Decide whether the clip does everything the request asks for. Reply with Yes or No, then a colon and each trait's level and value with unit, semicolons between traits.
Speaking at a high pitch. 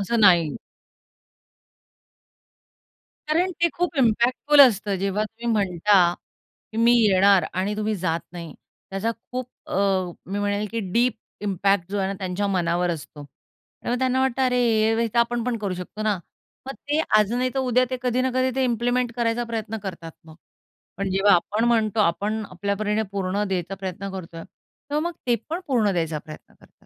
Yes: high, 210 Hz